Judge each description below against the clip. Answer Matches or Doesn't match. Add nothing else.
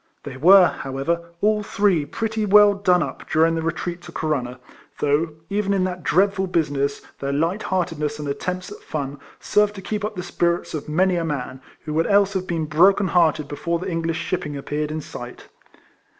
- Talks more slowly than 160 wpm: Doesn't match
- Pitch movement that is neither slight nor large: Matches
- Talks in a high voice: Doesn't match